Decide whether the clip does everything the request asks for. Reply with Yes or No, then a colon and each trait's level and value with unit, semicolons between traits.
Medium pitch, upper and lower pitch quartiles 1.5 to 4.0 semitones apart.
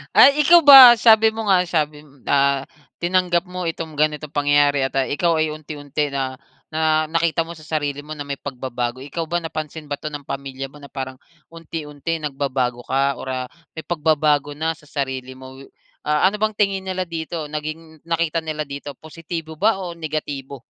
Yes: medium, 155 Hz; average, 2.8 semitones